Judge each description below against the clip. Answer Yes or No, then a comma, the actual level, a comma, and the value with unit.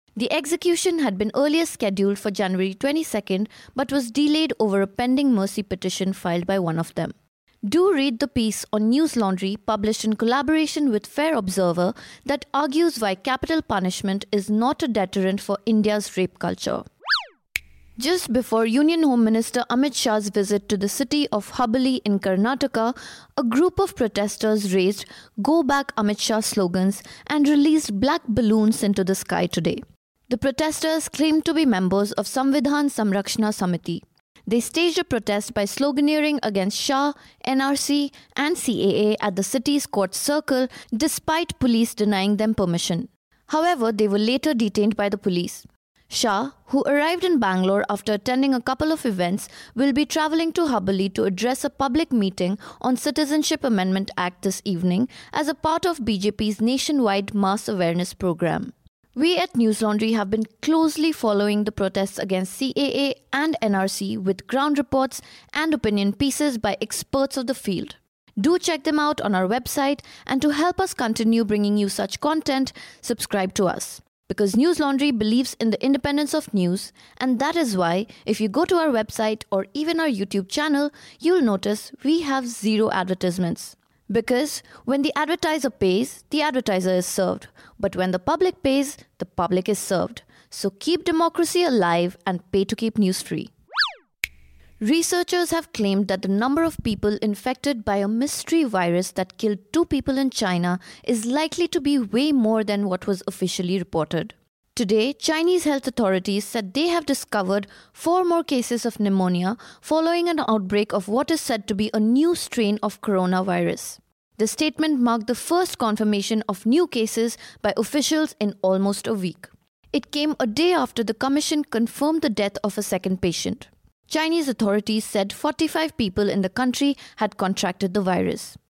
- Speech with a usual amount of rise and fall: No, wide, 6.3 semitones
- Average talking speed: Yes, average, 165 wpm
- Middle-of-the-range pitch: No, high, 230 Hz